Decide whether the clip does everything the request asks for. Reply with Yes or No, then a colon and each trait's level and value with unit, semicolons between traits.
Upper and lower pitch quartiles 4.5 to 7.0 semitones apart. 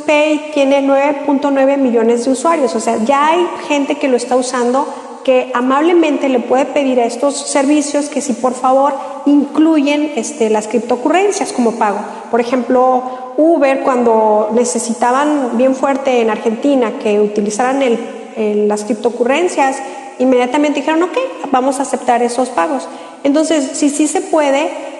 No: average, 3.1 semitones